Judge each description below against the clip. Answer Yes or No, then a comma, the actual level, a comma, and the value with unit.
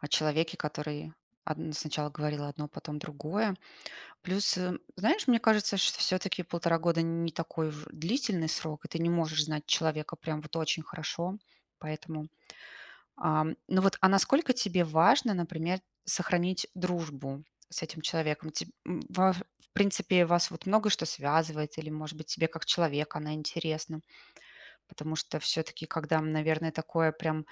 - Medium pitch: Yes, medium, 160 Hz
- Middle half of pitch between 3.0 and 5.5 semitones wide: No, narrow, 2.5 semitones